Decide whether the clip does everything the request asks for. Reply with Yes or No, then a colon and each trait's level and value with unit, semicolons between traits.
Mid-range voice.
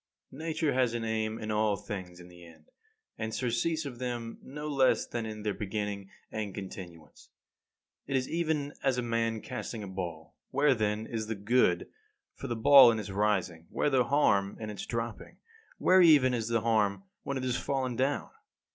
No: low, 115 Hz